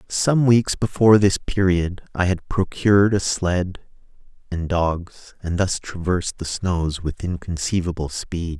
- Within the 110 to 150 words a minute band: Yes, average, 140 wpm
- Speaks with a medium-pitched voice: No, very low, 90 Hz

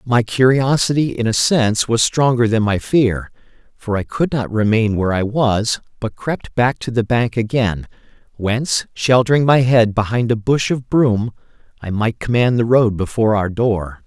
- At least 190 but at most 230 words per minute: No, average, 180 wpm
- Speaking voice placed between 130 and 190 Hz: No, low, 115 Hz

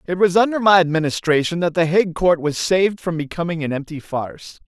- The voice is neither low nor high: Yes, medium, 170 Hz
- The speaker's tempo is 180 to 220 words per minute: Yes, fast, 205 wpm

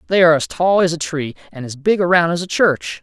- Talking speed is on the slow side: No, fast, 280 wpm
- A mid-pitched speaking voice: Yes, medium, 155 Hz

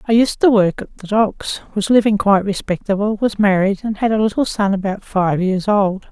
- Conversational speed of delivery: No, fast, 215 wpm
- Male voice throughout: No, female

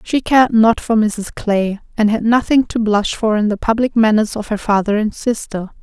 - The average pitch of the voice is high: Yes, high, 220 Hz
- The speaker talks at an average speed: No, fast, 215 wpm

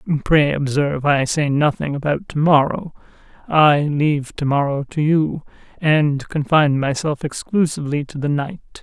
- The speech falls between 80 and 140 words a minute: Yes, slow, 135 wpm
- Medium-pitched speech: Yes, medium, 145 Hz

